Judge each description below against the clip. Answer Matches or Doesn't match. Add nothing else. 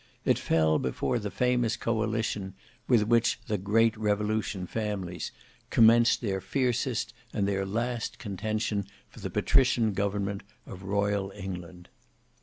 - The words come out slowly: Matches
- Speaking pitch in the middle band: Doesn't match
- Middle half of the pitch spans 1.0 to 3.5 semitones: Matches